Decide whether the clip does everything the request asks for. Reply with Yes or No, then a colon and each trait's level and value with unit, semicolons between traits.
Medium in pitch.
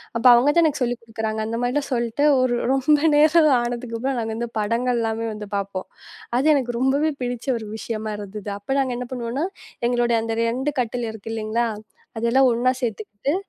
No: high, 235 Hz